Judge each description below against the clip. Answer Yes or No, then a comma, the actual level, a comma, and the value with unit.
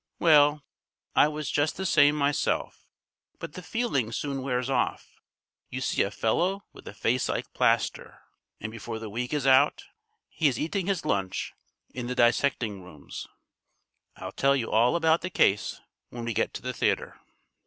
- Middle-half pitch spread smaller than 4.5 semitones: No, average, 4.8 semitones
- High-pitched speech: No, low, 130 Hz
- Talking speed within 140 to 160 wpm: No, average, 170 wpm